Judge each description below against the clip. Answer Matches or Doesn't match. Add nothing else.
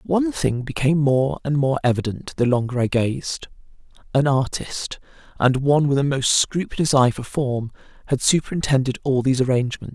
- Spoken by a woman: Matches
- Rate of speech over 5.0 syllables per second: Matches